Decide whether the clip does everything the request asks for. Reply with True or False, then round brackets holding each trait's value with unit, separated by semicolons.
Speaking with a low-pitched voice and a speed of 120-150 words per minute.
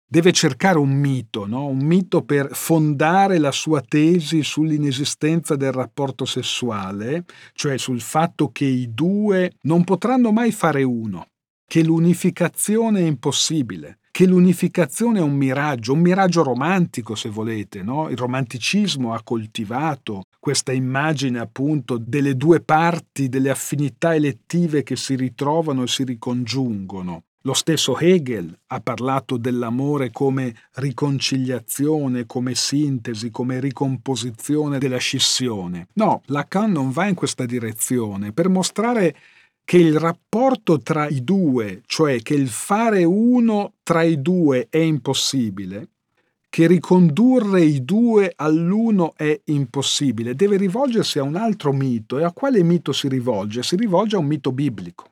False (145 Hz; 135 wpm)